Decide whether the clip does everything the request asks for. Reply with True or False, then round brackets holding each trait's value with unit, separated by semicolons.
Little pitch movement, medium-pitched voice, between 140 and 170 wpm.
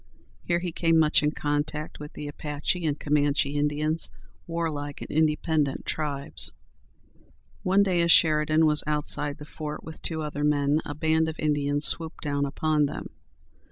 True (1.5 semitones; 150 Hz; 160 wpm)